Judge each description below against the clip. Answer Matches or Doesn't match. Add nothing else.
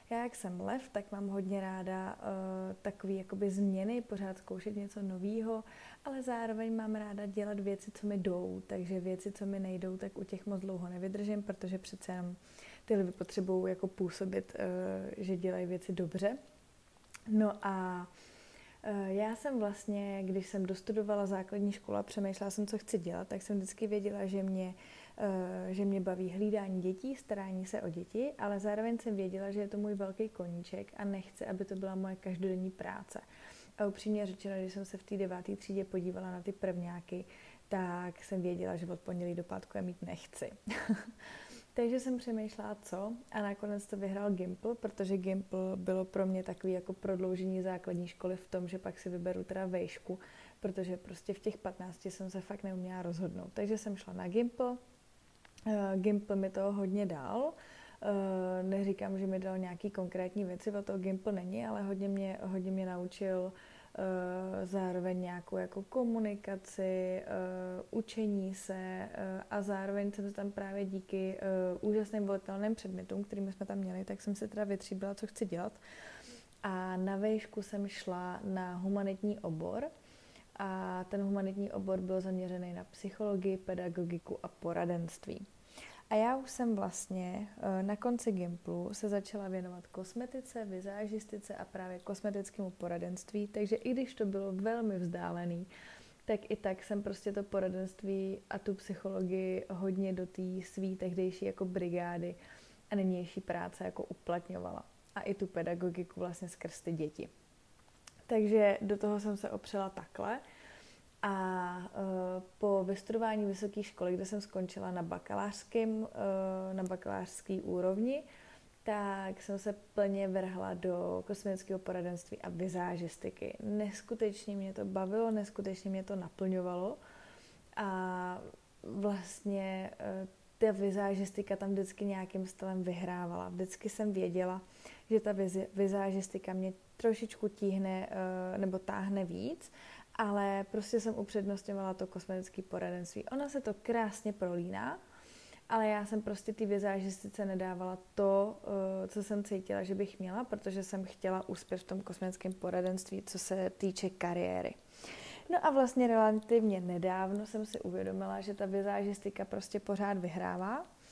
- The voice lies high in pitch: Matches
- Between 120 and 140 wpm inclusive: Doesn't match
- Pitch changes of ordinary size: Doesn't match